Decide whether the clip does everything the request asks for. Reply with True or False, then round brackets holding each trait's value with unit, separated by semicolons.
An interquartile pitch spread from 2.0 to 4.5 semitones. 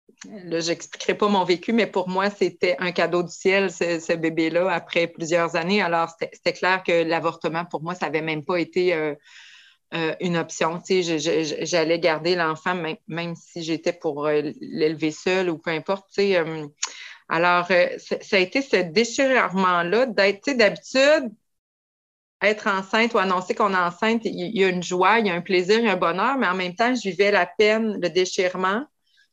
True (2.9 semitones)